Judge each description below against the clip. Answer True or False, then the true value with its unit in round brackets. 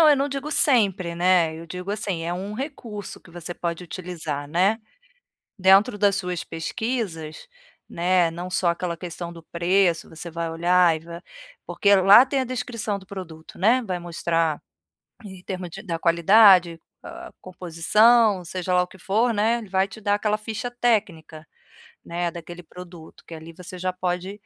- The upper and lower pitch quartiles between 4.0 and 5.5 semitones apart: False (3.5 semitones)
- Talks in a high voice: False (180 Hz)